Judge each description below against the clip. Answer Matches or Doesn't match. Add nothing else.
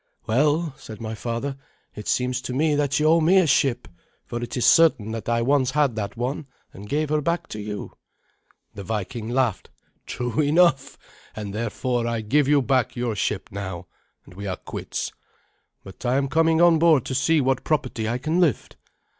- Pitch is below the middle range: Matches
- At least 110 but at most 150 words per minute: Doesn't match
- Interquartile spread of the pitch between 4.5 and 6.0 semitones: Matches